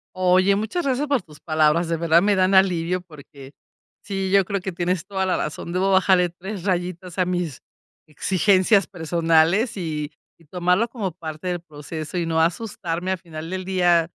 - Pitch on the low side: No, medium, 180 Hz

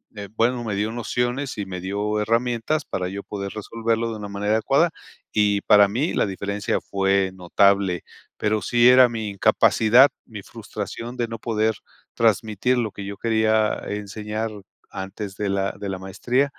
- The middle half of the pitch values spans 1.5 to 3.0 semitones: Yes, narrow, 2.6 semitones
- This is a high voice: No, low, 105 Hz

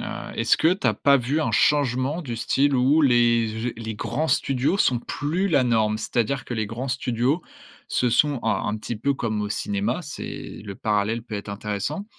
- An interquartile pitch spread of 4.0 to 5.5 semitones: Yes, average, 4.3 semitones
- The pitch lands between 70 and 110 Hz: No, low, 120 Hz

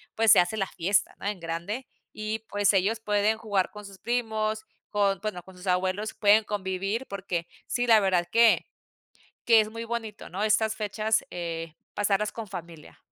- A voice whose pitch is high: Yes, high, 205 Hz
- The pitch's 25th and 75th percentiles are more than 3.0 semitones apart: No, average, 2.7 semitones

